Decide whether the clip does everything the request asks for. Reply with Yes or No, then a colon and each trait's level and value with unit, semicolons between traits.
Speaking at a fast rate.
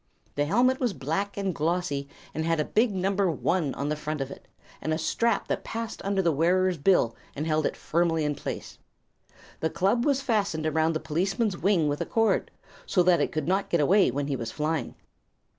Yes: fast, 210 wpm